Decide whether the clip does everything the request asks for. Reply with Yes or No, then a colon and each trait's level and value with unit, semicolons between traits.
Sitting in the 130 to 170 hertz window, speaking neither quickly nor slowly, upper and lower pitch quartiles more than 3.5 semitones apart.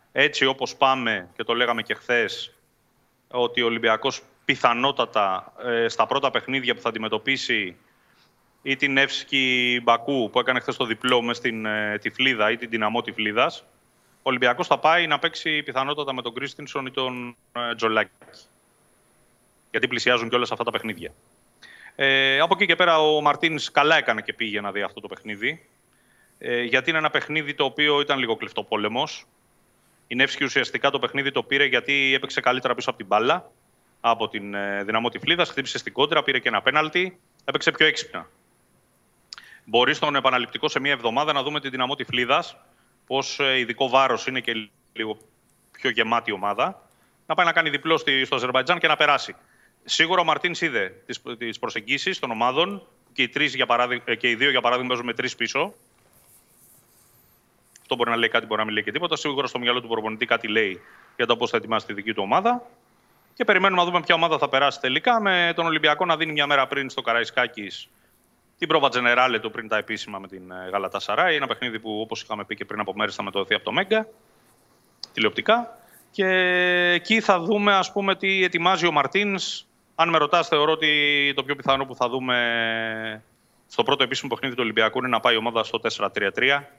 No: low, 135 Hz; fast, 185 wpm; average, 5.0 semitones